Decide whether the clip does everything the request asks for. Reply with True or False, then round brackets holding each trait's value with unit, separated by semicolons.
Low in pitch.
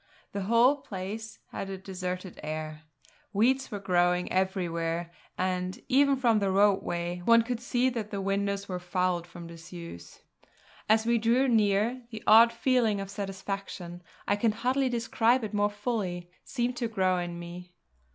False (200 Hz)